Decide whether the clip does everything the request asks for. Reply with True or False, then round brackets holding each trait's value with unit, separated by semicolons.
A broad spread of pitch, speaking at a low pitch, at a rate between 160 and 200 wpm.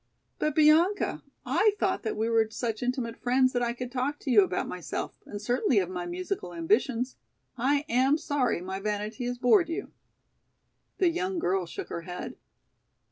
False (5.7 semitones; 245 Hz; 175 wpm)